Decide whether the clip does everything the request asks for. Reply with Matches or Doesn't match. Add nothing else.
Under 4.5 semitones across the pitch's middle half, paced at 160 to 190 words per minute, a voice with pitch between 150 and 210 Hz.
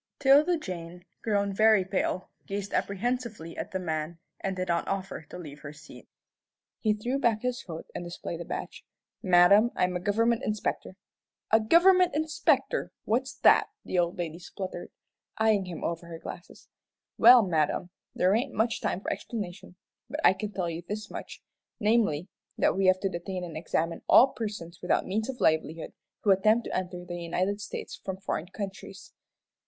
Matches